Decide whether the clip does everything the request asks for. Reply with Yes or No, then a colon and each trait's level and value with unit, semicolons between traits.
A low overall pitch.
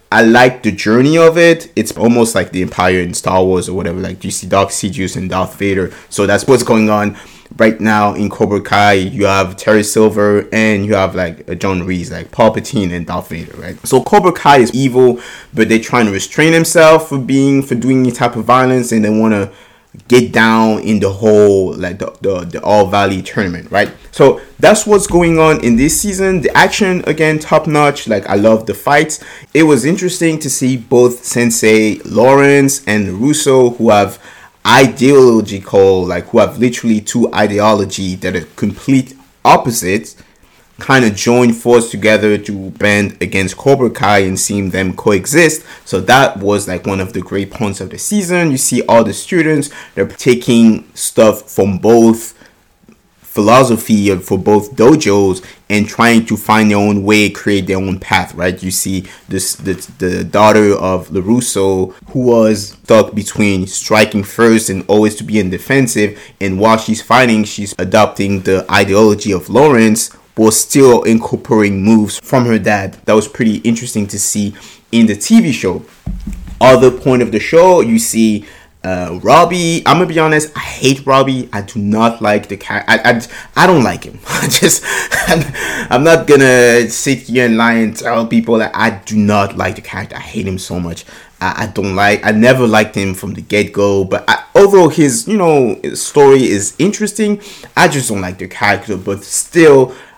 Yes: low, 110 Hz